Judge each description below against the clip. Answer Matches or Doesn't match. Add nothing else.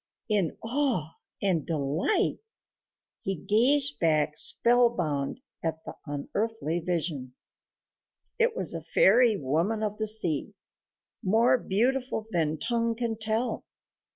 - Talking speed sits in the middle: Doesn't match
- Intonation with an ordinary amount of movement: Doesn't match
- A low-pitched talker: Doesn't match